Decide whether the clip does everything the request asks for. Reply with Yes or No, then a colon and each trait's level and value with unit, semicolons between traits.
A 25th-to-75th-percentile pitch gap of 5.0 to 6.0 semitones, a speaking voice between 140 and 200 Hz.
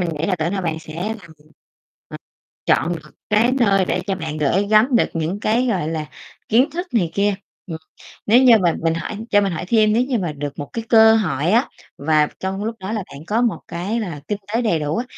Yes: wide, 5.5 semitones; high, 195 Hz